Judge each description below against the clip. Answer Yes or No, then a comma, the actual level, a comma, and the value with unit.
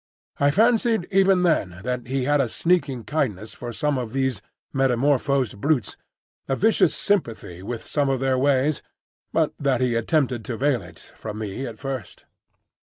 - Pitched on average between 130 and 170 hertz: Yes, low, 135 Hz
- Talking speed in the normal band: Yes, average, 165 wpm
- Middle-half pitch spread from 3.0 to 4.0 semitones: Yes, average, 3.7 semitones